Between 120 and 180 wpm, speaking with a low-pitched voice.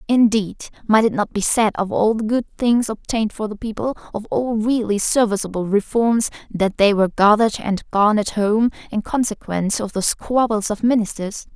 No: average, 175 wpm; high, 215 Hz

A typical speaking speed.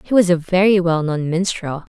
No: fast, 215 wpm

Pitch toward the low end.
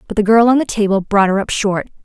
No: high, 210 Hz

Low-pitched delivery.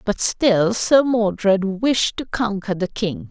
No: high, 205 Hz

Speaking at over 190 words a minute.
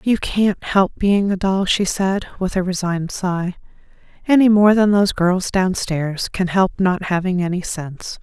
No: average, 175 wpm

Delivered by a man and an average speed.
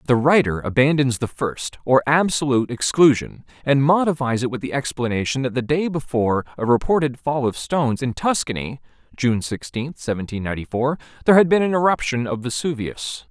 Yes: male; average, 165 wpm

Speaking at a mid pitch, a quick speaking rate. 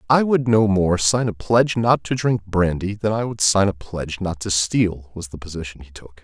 No: low, 100 Hz; fast, 240 wpm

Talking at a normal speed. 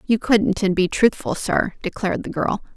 Yes: average, 195 wpm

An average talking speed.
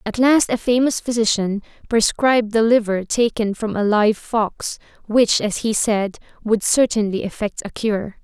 Yes: average, 160 wpm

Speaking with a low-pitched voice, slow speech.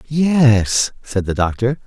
Yes: low, 125 Hz; slow, 130 wpm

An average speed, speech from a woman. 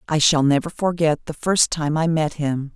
No: fast, 220 wpm; female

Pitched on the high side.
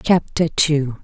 No: medium, 150 Hz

